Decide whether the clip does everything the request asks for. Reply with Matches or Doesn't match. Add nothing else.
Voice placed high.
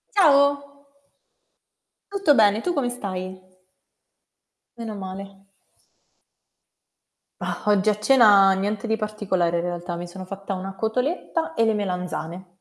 Matches